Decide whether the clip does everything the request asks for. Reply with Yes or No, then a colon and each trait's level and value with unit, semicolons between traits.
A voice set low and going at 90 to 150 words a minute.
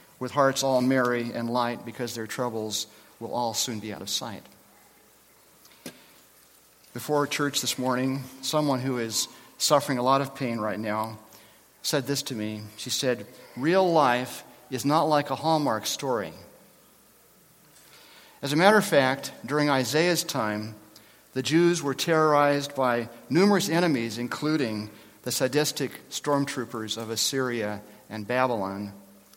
Yes: low, 125 Hz; slow, 135 wpm